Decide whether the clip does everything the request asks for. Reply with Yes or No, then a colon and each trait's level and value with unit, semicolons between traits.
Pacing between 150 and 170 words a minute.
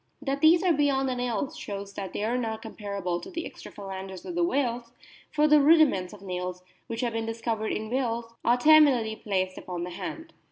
No: fast, 205 wpm